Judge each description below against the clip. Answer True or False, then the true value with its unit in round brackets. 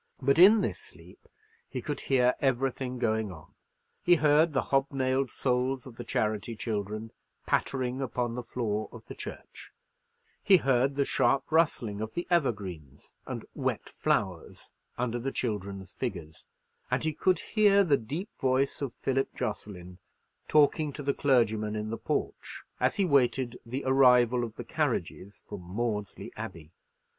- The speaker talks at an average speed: True (150 wpm)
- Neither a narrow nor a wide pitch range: True (4.2 semitones)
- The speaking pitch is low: True (125 Hz)